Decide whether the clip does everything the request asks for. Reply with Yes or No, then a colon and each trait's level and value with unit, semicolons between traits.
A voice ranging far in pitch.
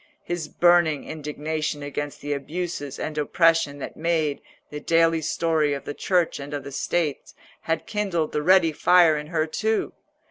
No: narrow, 2.5 semitones